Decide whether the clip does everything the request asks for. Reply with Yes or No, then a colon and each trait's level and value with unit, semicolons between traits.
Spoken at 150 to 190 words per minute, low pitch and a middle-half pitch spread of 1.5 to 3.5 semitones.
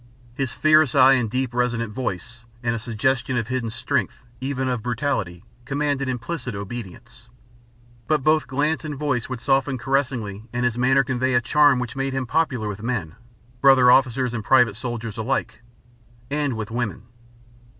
Yes: average, 160 wpm; low, 125 Hz; average, 2.7 semitones